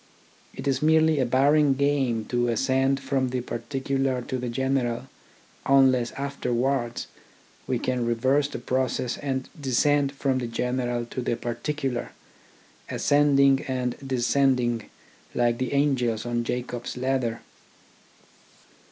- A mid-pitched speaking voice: No, low, 130 Hz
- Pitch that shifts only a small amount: Yes, narrow, 2.2 semitones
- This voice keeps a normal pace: No, slow, 125 wpm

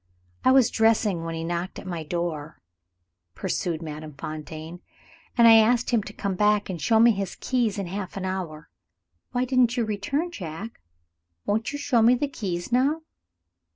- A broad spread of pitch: Yes, wide, 5.7 semitones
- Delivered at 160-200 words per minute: Yes, average, 175 wpm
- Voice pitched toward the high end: Yes, high, 200 Hz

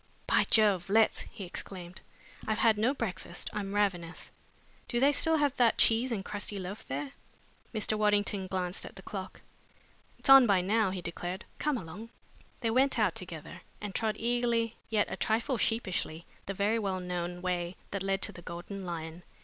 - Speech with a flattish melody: No, average, 3.9 semitones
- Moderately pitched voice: No, high, 200 Hz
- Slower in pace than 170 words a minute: No, average, 175 wpm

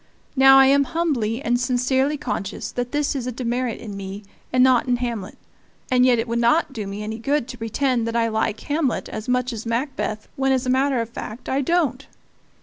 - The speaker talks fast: Yes, fast, 215 wpm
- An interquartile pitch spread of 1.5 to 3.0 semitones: Yes, average, 2.7 semitones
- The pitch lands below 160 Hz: No, very high, 250 Hz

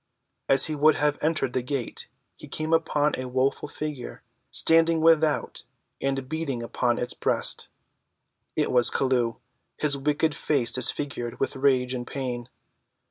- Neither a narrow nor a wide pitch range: Yes, average, 3.2 semitones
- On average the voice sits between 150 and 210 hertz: No, low, 135 Hz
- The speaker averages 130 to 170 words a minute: Yes, average, 140 wpm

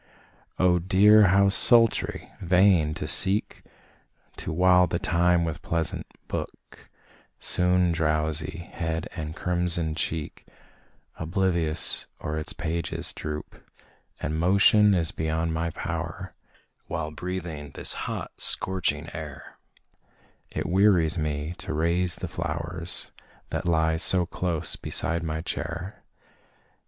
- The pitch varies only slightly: Yes, narrow, 2.3 semitones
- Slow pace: Yes, slow, 115 wpm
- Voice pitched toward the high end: No, very low, 85 Hz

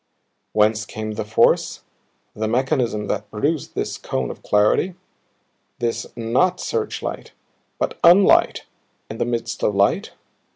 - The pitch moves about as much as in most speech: Yes, average, 4.1 semitones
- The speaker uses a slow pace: Yes, slow, 125 wpm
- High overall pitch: No, low, 115 Hz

